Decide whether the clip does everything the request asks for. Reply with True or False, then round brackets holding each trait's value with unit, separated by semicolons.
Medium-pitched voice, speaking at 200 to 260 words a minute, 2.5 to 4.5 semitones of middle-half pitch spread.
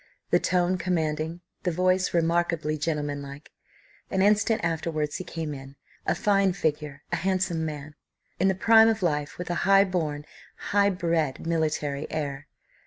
False (165 Hz; 150 wpm; 3.6 semitones)